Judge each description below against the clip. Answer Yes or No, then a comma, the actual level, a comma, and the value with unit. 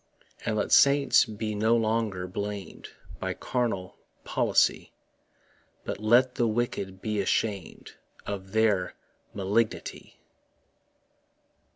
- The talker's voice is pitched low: Yes, low, 110 Hz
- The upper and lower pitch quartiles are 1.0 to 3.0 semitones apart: Yes, average, 2.7 semitones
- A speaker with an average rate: No, slow, 95 wpm